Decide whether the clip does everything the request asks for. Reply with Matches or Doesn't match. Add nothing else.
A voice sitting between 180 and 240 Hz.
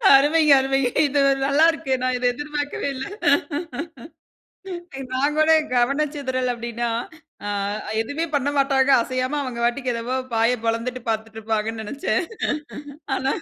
Doesn't match